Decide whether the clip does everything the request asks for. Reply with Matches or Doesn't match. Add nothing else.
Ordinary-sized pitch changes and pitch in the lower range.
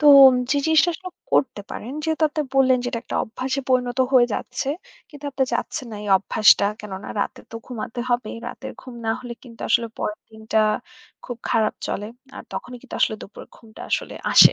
Doesn't match